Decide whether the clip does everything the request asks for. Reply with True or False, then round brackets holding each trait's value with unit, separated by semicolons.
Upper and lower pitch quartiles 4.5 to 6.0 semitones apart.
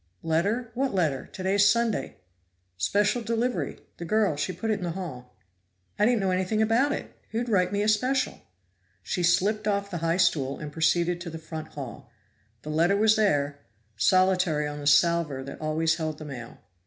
True (5.4 semitones)